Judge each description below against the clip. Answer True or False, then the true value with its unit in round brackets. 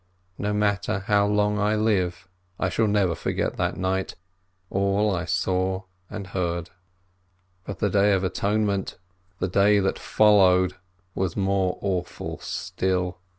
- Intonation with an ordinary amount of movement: False (2.0 semitones)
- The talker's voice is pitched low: True (95 Hz)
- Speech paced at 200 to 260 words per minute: False (140 wpm)